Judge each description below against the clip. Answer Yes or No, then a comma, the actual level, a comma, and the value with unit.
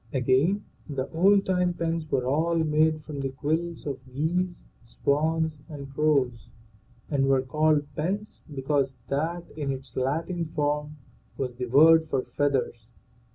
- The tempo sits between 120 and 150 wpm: Yes, average, 140 wpm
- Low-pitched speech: No, medium, 150 Hz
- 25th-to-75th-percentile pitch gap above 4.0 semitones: No, average, 3.2 semitones